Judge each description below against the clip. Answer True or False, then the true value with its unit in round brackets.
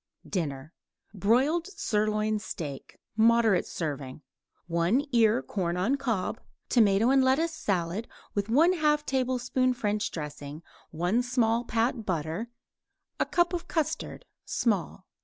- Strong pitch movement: True (6.4 semitones)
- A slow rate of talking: True (105 wpm)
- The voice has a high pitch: True (220 Hz)